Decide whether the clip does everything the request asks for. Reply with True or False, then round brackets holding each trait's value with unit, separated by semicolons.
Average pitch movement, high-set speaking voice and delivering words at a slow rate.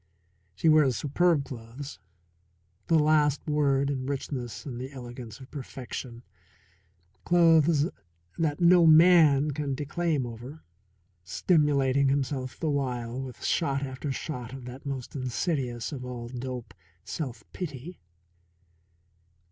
False (3.2 semitones; 140 Hz; 115 wpm)